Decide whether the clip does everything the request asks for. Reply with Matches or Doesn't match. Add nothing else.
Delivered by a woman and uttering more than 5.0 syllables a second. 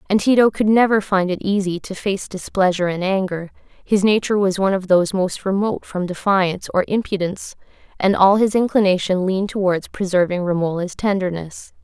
Matches